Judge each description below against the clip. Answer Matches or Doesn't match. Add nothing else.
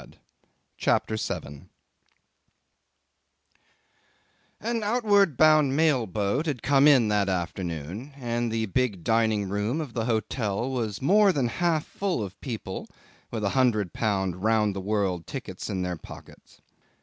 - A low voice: Matches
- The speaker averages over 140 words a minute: Doesn't match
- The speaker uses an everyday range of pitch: Doesn't match